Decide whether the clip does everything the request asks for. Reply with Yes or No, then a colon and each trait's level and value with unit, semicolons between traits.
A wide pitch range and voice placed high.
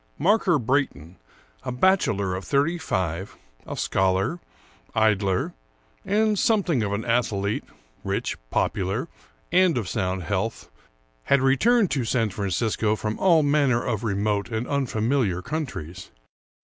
No: wide, 6.6 semitones; low, 115 Hz